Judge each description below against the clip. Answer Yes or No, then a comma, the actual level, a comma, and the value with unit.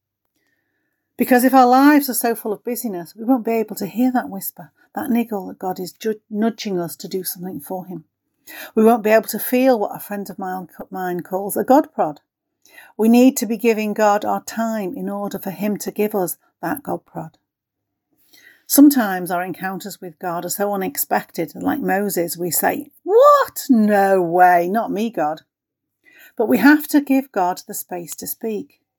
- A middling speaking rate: Yes, average, 185 wpm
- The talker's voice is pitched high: Yes, high, 210 Hz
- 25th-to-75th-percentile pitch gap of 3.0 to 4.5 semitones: No, average, 5.1 semitones